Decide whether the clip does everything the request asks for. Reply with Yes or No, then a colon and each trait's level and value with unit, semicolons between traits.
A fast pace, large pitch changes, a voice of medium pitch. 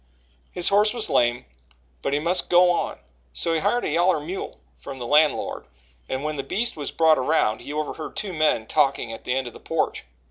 No: fast, 210 wpm; average, 4.6 semitones; medium, 155 Hz